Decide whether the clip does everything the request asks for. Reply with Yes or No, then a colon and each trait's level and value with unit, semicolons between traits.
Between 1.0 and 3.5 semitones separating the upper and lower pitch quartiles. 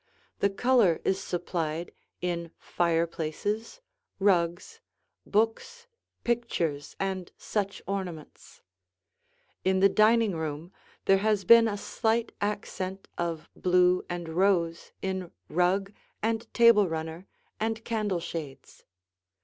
No: average, 3.9 semitones